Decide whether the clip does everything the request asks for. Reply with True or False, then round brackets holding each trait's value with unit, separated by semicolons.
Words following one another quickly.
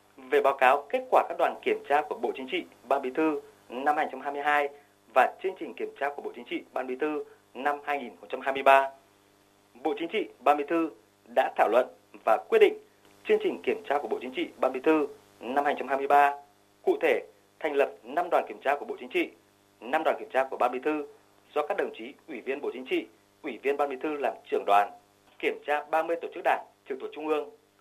False (225 wpm)